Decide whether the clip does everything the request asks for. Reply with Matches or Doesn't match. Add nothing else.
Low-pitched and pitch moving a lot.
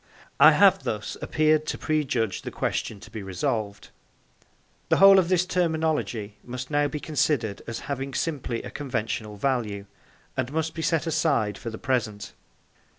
Matches